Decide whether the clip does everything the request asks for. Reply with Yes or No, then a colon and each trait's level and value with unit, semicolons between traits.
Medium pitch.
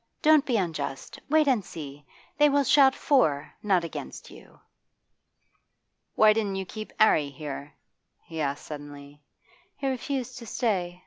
No: high, 195 Hz